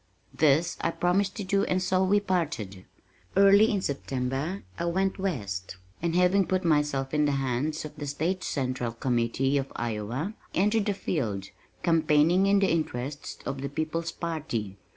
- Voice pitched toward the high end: No, medium, 155 Hz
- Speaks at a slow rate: No, average, 160 wpm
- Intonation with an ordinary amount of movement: No, wide, 5.7 semitones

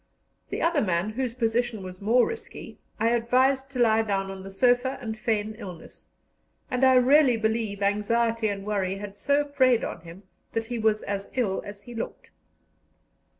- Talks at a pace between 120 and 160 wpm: No, average, 175 wpm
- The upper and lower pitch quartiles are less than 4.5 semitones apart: Yes, average, 3.7 semitones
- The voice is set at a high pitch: Yes, high, 225 Hz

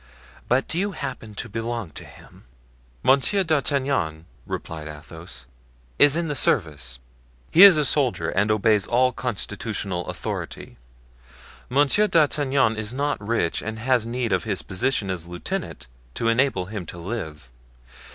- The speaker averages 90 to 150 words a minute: Yes, average, 140 wpm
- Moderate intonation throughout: No, wide, 7.1 semitones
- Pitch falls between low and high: No, low, 115 Hz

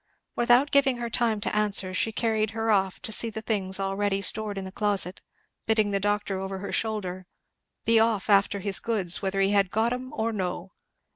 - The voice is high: Yes, high, 205 Hz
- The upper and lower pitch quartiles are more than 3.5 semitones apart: No, narrow, 2.4 semitones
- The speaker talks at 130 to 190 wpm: No, average, 200 wpm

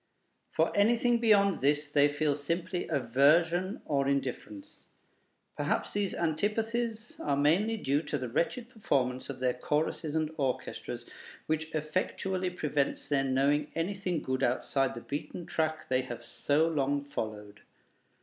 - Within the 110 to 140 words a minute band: Yes, slow, 135 wpm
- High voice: No, medium, 150 Hz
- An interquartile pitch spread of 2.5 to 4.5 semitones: No, average, 4.9 semitones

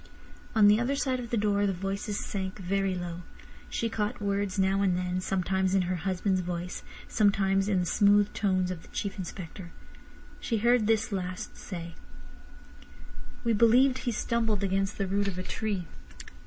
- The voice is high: Yes, high, 195 Hz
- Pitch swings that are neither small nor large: No, narrow, 2.3 semitones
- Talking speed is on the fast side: No, average, 170 wpm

